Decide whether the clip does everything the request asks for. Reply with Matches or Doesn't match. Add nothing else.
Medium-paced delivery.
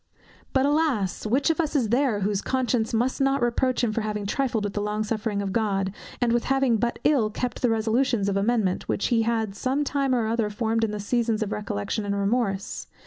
Doesn't match